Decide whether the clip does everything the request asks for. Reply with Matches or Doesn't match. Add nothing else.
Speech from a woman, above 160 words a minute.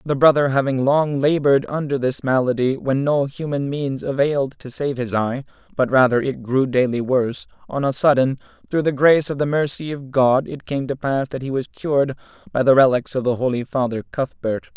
Doesn't match